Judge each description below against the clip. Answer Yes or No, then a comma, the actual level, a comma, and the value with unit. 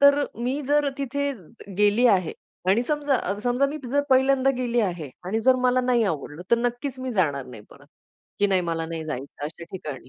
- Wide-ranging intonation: Yes, wide, 8.4 semitones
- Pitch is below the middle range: No, high, 235 Hz